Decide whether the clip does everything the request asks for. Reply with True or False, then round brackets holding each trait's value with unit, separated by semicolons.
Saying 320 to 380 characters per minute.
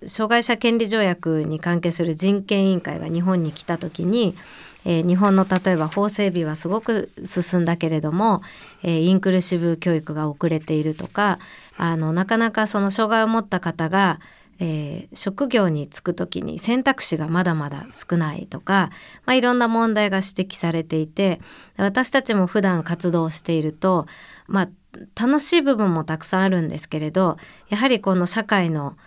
True (330 characters per minute)